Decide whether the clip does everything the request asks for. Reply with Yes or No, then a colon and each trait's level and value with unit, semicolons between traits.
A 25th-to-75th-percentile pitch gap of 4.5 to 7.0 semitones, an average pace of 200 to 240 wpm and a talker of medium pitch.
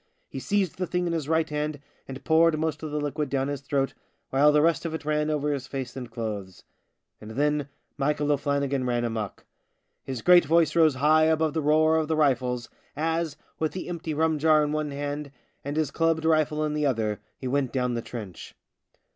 No: average, 2.8 semitones; fast, 205 wpm; medium, 150 Hz